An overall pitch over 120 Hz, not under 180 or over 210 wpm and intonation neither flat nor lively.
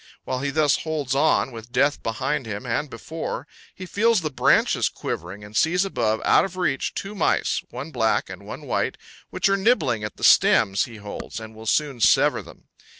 No: low, 135 Hz; average, 195 wpm; wide, 6.2 semitones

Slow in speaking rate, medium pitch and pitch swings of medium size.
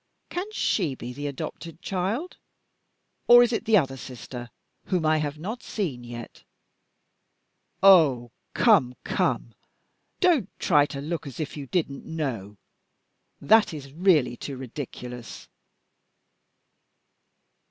No: slow, 120 wpm; medium, 150 Hz; wide, 6.9 semitones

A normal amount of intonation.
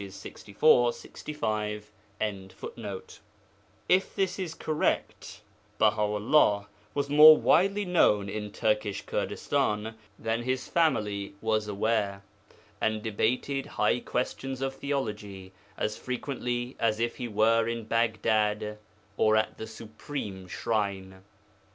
Yes: average, 3.6 semitones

